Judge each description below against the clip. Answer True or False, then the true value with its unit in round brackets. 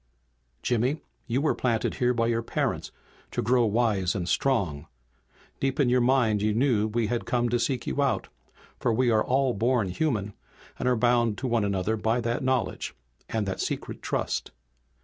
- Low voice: True (120 Hz)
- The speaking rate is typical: True (185 wpm)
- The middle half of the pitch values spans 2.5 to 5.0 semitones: True (2.8 semitones)